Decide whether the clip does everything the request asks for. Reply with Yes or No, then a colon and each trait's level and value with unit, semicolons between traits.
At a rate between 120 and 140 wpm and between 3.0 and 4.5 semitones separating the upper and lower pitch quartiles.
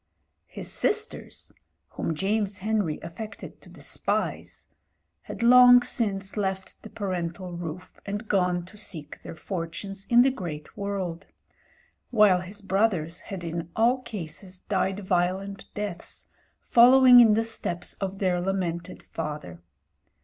Yes: slow, 135 wpm; average, 3.4 semitones